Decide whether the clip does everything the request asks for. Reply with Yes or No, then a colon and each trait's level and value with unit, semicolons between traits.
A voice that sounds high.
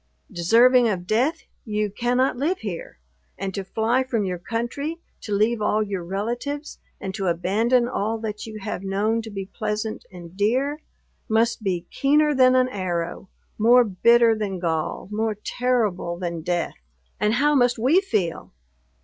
Yes: high, 215 Hz